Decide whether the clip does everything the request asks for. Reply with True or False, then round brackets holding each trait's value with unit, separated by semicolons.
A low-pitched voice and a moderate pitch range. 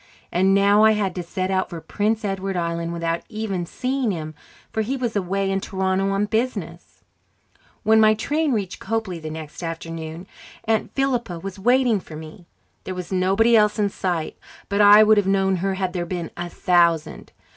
False (195 Hz; 3.8 semitones)